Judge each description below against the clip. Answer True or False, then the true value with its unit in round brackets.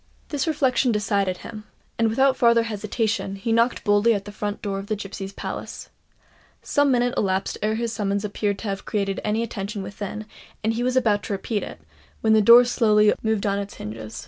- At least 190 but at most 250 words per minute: True (200 wpm)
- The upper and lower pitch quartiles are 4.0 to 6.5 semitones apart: False (2.6 semitones)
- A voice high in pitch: True (210 Hz)